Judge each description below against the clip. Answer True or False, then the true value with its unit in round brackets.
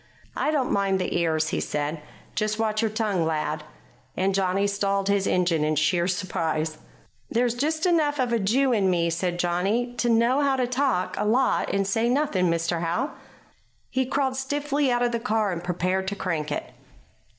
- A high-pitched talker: True (200 Hz)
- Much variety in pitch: True (5.9 semitones)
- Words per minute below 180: False (185 wpm)